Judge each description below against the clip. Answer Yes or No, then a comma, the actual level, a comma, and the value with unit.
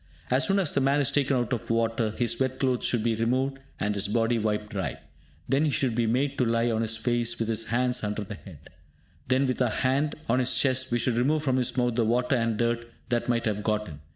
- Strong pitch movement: No, narrow, 2.4 semitones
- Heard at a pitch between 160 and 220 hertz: No, low, 120 Hz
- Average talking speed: No, fast, 250 wpm